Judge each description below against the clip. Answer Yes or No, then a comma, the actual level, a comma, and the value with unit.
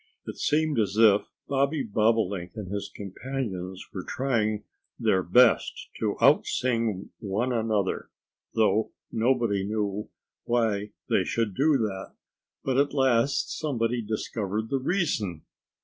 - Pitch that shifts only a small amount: No, average, 4.0 semitones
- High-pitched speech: No, low, 110 Hz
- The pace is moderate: No, slow, 125 wpm